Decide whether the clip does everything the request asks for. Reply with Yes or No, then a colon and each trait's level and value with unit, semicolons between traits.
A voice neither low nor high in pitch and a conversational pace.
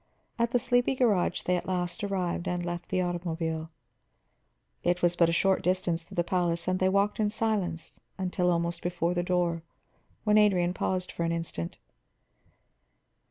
Yes: medium, 180 Hz; average, 165 wpm